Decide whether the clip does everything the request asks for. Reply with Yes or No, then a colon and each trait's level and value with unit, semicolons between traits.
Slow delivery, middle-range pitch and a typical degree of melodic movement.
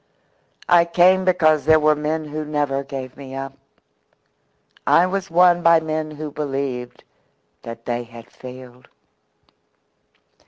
Yes: slow, 125 wpm; medium, 150 Hz; average, 3.8 semitones